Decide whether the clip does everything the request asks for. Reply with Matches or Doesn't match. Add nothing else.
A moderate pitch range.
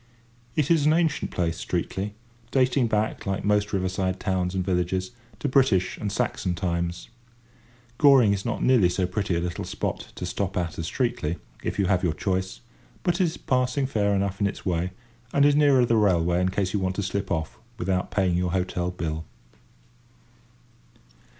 Matches